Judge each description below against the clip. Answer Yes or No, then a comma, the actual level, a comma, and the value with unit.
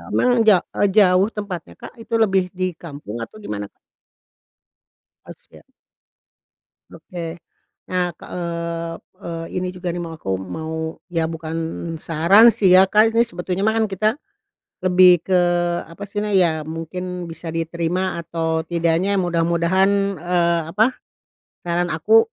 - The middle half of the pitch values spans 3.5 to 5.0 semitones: No, narrow, 2.5 semitones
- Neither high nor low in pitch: Yes, medium, 175 Hz